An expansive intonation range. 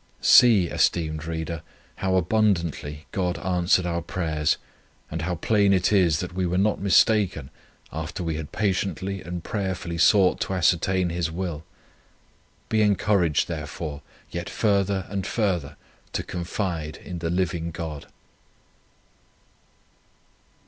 No: average, 2.8 semitones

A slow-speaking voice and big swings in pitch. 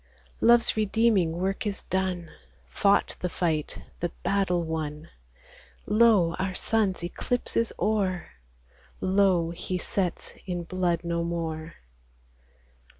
No: slow, 110 wpm; average, 2.9 semitones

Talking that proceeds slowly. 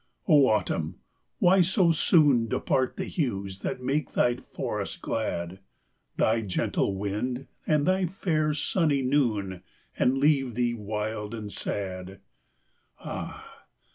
Yes: slow, 120 wpm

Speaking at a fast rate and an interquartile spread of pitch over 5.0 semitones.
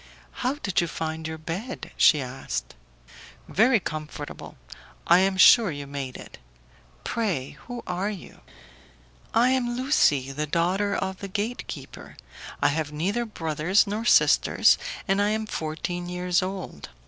No: average, 145 wpm; wide, 5.4 semitones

